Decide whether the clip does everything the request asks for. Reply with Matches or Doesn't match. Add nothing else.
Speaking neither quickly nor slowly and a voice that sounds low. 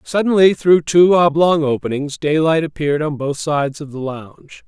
Doesn't match